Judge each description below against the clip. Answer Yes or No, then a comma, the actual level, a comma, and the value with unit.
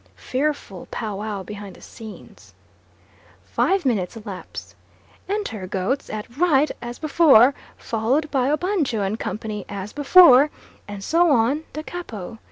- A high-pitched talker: Yes, high, 240 Hz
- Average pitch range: No, wide, 6.4 semitones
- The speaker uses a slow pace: Yes, slow, 130 wpm